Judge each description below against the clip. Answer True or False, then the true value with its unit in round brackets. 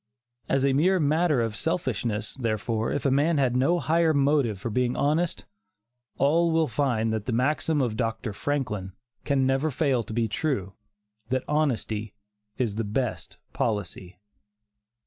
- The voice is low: True (130 Hz)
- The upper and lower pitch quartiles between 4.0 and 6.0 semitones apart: True (5.1 semitones)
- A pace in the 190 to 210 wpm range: False (150 wpm)